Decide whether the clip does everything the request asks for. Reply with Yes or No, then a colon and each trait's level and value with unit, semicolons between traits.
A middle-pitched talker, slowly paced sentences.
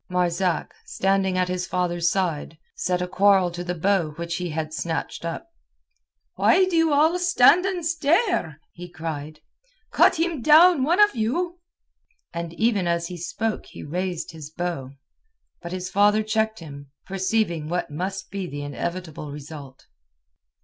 No: medium, 180 Hz; average, 155 wpm